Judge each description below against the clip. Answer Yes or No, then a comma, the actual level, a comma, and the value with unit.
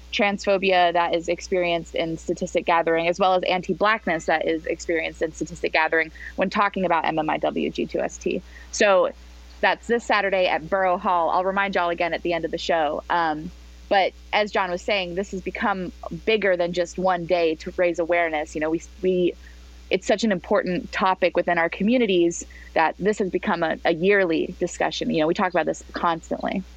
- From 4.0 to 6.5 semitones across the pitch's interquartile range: No, narrow, 2.5 semitones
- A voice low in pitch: No, medium, 175 Hz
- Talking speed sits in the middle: Yes, average, 185 wpm